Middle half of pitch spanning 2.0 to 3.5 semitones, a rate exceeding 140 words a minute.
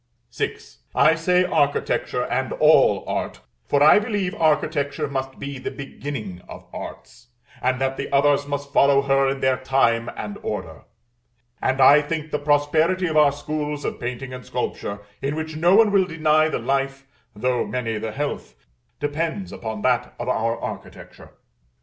Yes: average, 2.8 semitones; average, 160 wpm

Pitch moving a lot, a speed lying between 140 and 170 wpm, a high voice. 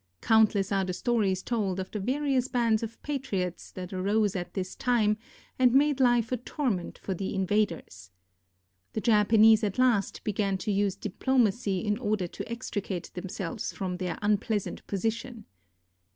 No: average, 3.6 semitones; average, 150 wpm; high, 210 Hz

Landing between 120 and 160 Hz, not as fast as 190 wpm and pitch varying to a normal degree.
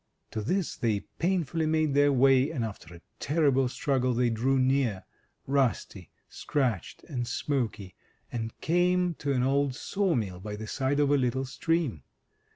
Yes: low, 135 Hz; average, 165 wpm; average, 4.1 semitones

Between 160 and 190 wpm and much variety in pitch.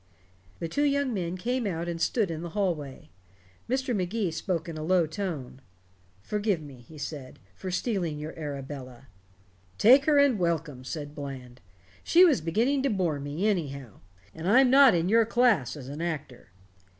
Yes: average, 170 wpm; wide, 7.0 semitones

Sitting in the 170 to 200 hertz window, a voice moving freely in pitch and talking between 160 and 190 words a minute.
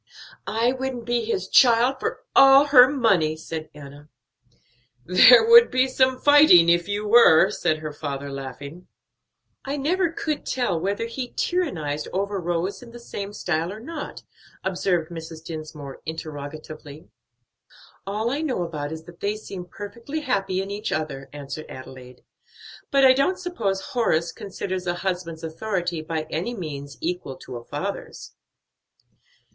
No: medium, 185 Hz; wide, 7.4 semitones; average, 150 wpm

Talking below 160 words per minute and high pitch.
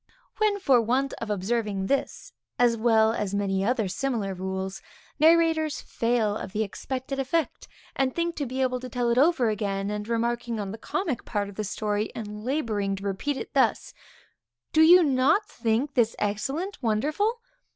No: average, 170 wpm; high, 235 Hz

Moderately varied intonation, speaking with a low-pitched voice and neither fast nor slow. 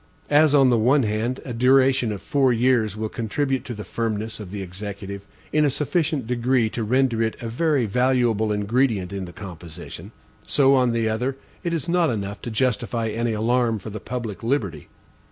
Yes: average, 3.5 semitones; low, 115 Hz; average, 190 wpm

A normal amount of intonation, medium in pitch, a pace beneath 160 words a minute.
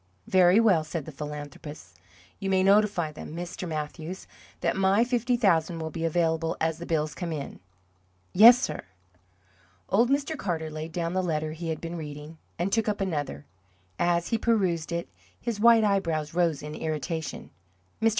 No: average, 3.9 semitones; medium, 170 Hz; average, 170 wpm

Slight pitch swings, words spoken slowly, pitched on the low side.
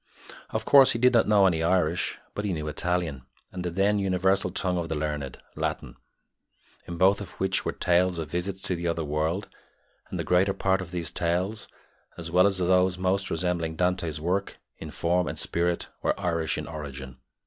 No: narrow, 2.3 semitones; average, 190 wpm; very low, 90 Hz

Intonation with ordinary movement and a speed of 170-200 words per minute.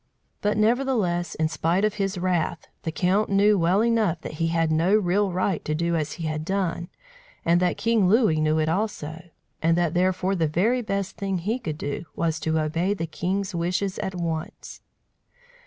Yes: average, 3.5 semitones; average, 190 wpm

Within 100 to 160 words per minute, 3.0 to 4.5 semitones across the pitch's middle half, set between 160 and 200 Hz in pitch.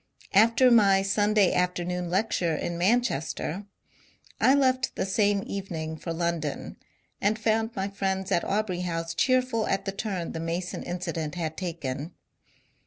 Yes: average, 140 wpm; average, 3.9 semitones; high, 190 Hz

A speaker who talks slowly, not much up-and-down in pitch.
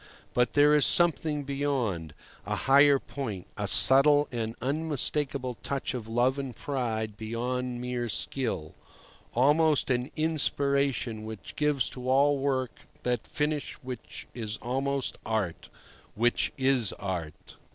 No: slow, 120 wpm; average, 3.6 semitones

